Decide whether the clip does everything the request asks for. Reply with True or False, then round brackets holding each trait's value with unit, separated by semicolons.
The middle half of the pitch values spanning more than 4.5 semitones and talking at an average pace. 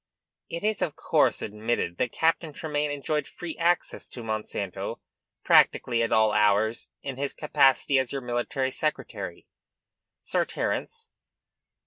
False (5.3 semitones; 130 wpm)